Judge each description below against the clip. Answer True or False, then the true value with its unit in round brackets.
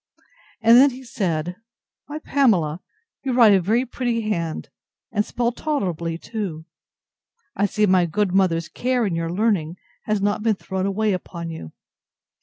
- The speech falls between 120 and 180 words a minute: True (155 wpm)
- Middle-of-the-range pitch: False (200 Hz)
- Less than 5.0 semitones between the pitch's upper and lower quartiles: False (5.3 semitones)